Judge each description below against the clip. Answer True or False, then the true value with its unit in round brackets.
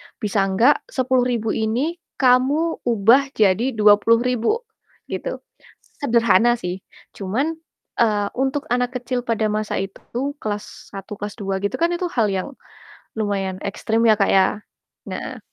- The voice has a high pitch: True (230 Hz)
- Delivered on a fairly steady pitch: False (3.8 semitones)